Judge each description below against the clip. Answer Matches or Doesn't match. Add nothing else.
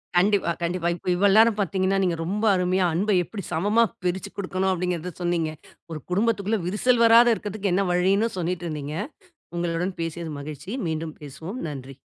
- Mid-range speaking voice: Matches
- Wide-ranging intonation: Doesn't match